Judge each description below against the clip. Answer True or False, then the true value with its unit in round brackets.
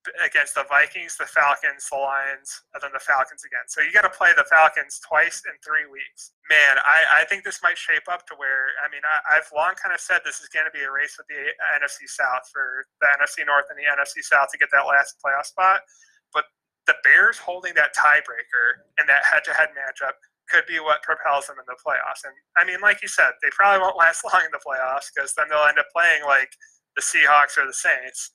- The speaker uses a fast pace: True (235 wpm)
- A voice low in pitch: False (175 Hz)